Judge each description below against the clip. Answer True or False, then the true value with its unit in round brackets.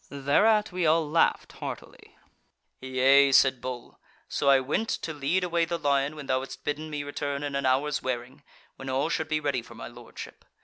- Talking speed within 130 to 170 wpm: False (190 wpm)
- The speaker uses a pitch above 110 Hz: True (140 Hz)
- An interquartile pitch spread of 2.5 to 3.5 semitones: True (2.9 semitones)